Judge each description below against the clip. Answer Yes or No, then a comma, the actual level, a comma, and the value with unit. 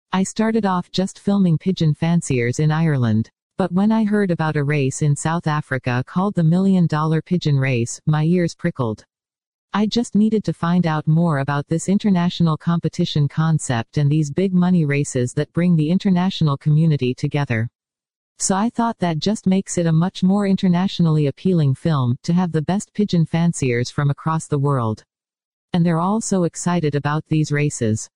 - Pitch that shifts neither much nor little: Yes, average, 3.9 semitones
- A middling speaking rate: Yes, average, 175 wpm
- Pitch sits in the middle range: Yes, medium, 165 Hz